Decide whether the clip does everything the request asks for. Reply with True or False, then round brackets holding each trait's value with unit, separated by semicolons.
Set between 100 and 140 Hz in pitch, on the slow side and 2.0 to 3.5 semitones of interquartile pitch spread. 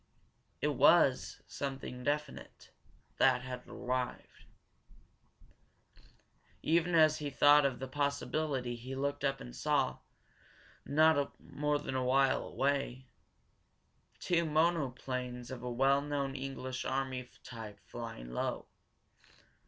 True (135 Hz; 110 wpm; 2.4 semitones)